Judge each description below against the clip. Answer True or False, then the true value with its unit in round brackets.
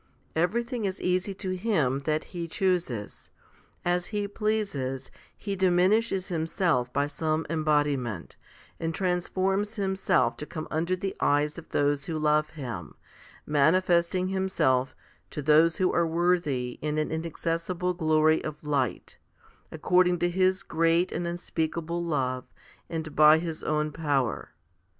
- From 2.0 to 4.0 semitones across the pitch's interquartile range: True (3.5 semitones)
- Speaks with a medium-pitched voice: True (165 Hz)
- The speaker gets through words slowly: True (130 wpm)